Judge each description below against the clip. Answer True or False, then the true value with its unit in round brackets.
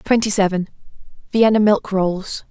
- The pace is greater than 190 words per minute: False (95 wpm)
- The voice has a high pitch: True (200 Hz)